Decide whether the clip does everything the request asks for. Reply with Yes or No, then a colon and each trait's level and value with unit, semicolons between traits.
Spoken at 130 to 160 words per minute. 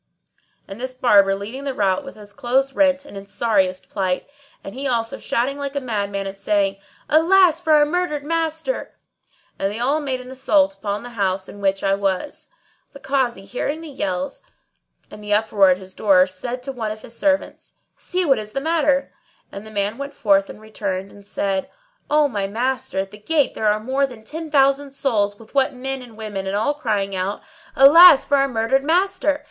No: average, 200 wpm